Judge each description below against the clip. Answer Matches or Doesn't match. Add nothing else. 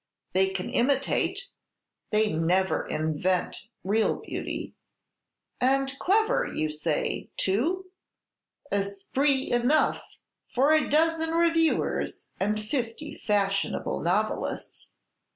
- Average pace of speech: Doesn't match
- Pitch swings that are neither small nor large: Doesn't match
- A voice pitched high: Matches